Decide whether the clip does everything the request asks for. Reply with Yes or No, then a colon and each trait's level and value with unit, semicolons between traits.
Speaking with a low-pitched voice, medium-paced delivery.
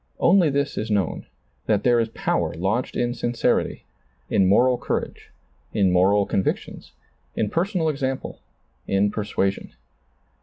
No: low, 110 Hz; slow, 125 wpm